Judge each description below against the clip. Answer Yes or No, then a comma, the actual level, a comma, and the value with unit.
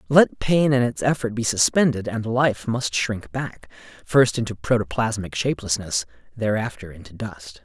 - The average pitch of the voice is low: Yes, low, 110 Hz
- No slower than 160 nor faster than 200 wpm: No, average, 150 wpm